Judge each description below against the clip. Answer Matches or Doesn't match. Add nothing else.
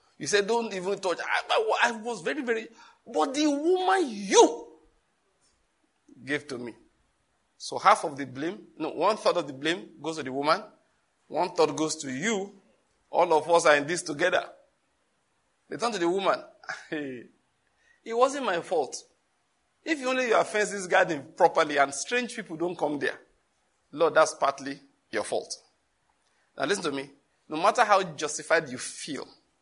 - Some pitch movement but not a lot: Doesn't match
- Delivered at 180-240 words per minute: Doesn't match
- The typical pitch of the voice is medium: Matches